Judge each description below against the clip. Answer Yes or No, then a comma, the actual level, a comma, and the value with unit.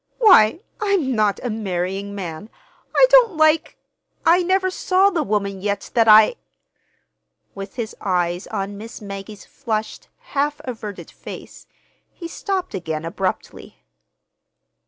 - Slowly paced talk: Yes, slow, 120 wpm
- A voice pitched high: Yes, high, 215 Hz